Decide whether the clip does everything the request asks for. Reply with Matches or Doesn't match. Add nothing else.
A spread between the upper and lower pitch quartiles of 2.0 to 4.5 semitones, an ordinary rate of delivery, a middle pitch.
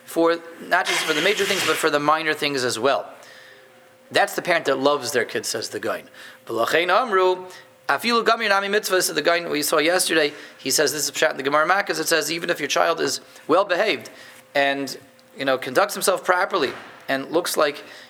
Matches